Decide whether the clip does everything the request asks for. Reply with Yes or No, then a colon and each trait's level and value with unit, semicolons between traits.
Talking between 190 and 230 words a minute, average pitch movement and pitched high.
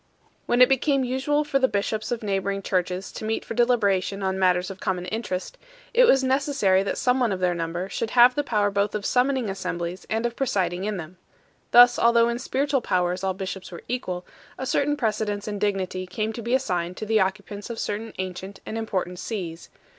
Yes: fast, 205 wpm; average, 4.6 semitones; high, 205 Hz